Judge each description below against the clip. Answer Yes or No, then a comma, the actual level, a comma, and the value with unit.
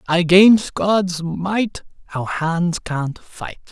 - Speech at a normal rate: No, slow, 115 wpm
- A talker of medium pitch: Yes, medium, 180 Hz